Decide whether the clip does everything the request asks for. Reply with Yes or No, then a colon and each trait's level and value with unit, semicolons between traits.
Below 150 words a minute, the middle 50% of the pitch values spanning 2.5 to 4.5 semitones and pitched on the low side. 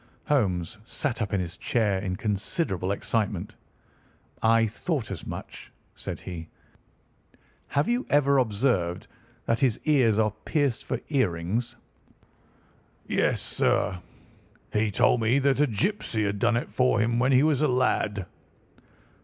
No: slow, 135 wpm; average, 5.0 semitones; low, 115 Hz